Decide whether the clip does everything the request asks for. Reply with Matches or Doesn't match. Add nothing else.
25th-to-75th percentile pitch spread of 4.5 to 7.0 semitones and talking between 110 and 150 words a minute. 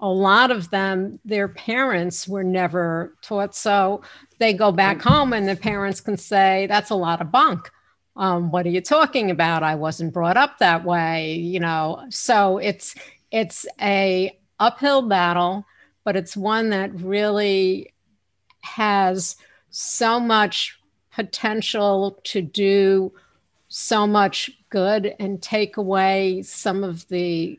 Doesn't match